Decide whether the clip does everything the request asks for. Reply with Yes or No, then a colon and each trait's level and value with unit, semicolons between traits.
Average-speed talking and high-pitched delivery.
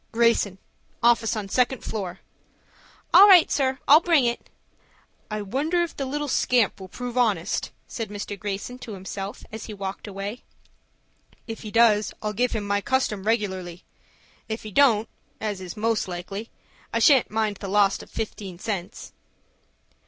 Yes: average, 155 wpm; high, 215 Hz